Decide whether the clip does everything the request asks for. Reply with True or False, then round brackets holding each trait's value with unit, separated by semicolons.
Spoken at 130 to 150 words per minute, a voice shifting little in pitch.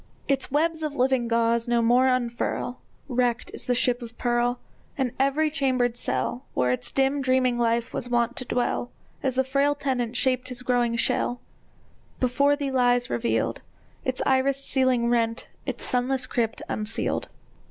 False (160 wpm; 1.8 semitones)